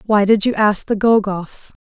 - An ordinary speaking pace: Yes, average, 195 wpm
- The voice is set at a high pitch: Yes, high, 205 Hz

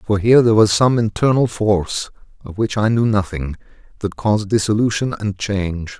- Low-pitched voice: Yes, low, 105 Hz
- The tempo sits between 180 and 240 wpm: No, average, 170 wpm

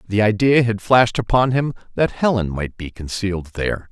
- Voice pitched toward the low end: Yes, low, 110 Hz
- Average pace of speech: Yes, average, 185 wpm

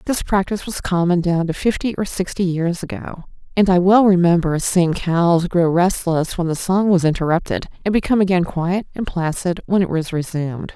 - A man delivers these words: No, female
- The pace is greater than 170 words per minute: Yes, average, 190 wpm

